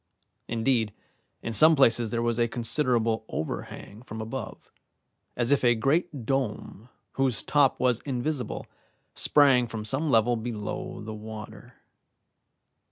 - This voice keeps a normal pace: No, slow, 125 wpm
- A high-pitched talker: No, low, 120 Hz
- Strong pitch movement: No, average, 3.2 semitones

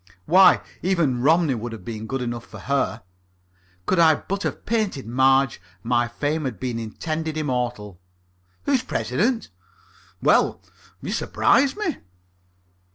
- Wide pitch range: Yes, wide, 6.6 semitones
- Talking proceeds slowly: Yes, slow, 130 wpm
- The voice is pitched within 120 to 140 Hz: Yes, low, 135 Hz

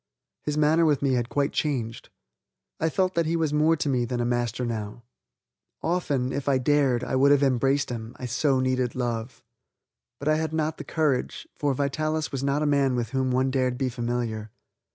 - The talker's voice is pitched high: No, low, 135 Hz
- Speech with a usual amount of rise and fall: Yes, average, 3.3 semitones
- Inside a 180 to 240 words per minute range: Yes, average, 200 wpm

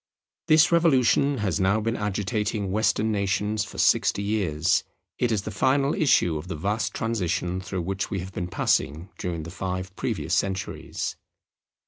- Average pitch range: Yes, average, 3.3 semitones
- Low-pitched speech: Yes, low, 100 Hz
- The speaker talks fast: No, average, 155 wpm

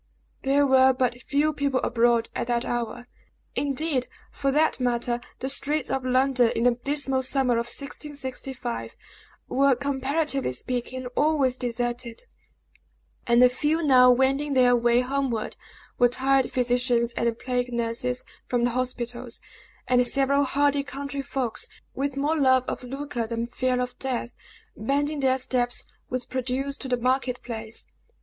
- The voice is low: No, very high, 255 Hz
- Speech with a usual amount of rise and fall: No, narrow, 2.2 semitones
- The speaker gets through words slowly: No, average, 145 wpm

